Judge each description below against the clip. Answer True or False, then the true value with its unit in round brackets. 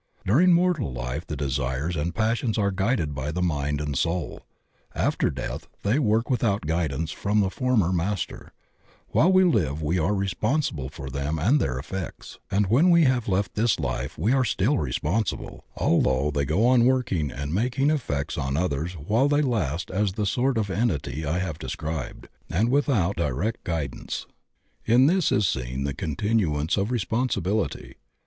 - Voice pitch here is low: True (95 Hz)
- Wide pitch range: True (7.9 semitones)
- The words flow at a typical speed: True (170 wpm)